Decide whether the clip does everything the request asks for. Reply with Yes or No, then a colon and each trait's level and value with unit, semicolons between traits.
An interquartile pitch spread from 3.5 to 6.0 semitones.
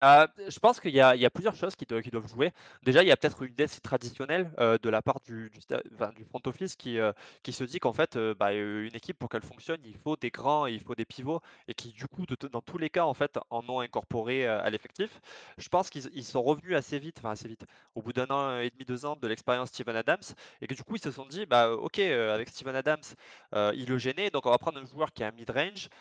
Yes: average, 4.7 semitones